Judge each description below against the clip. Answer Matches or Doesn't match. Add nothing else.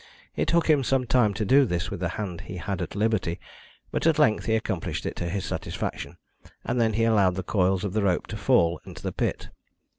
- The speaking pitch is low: Matches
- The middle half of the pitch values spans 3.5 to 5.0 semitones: Matches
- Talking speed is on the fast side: Matches